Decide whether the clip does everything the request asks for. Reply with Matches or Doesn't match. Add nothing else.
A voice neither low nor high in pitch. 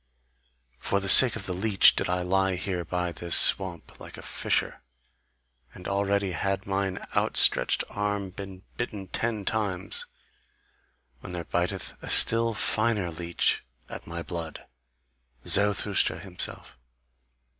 Doesn't match